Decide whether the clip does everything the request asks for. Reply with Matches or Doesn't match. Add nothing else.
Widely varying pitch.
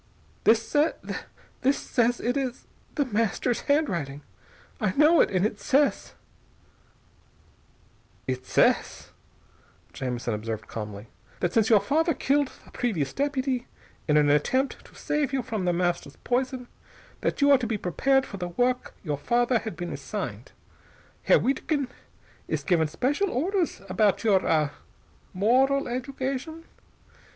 Matches